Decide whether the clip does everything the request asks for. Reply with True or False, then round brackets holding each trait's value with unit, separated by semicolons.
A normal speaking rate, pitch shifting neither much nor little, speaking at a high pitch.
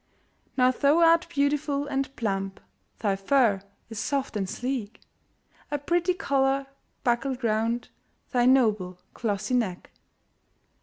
False (115 wpm; 4.6 semitones; 255 Hz)